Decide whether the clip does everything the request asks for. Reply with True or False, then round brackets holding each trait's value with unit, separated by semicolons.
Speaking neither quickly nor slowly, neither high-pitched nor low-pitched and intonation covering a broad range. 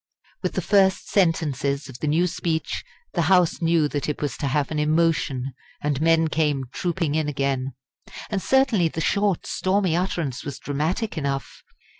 False (165 wpm; 160 Hz; 3.8 semitones)